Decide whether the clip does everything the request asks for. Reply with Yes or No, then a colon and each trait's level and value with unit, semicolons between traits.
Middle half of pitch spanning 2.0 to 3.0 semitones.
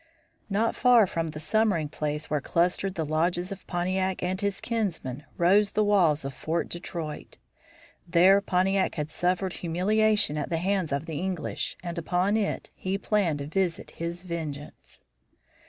No: average, 3.5 semitones